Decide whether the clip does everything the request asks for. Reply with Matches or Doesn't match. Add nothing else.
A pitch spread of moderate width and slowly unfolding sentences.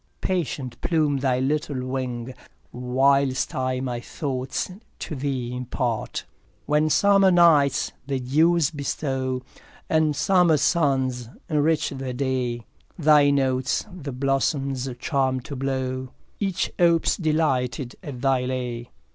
Matches